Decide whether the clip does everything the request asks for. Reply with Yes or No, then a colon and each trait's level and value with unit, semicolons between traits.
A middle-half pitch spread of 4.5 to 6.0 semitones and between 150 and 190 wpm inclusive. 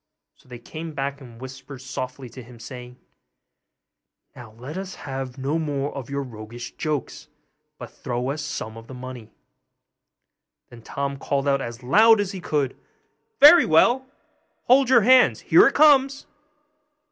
Yes: average, 4.8 semitones; average, 160 wpm